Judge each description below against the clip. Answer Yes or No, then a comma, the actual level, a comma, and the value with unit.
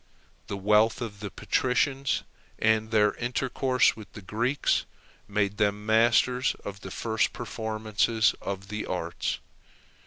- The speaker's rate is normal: No, slow, 125 wpm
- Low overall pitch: Yes, low, 110 Hz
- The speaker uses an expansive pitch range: No, narrow, 2.4 semitones